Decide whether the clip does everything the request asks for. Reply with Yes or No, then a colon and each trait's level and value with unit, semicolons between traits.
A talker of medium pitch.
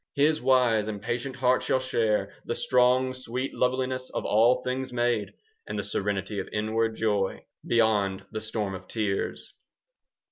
No: low, 115 Hz